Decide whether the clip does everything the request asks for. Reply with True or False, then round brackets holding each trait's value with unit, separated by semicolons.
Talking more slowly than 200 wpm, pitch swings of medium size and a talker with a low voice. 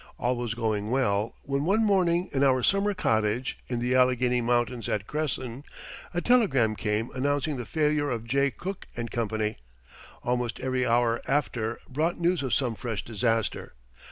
True (160 wpm; 3.9 semitones; 125 Hz)